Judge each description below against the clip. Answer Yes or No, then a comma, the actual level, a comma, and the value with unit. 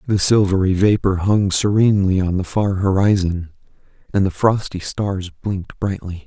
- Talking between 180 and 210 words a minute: No, average, 145 wpm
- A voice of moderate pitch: No, very low, 95 Hz